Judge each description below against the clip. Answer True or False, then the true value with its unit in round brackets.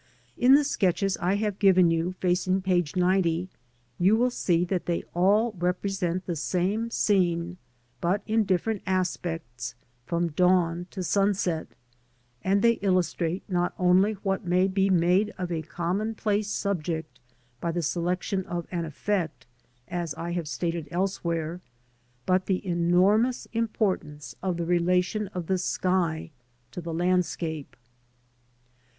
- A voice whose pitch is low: False (180 Hz)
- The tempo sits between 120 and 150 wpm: True (140 wpm)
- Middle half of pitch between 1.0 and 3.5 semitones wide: True (2.4 semitones)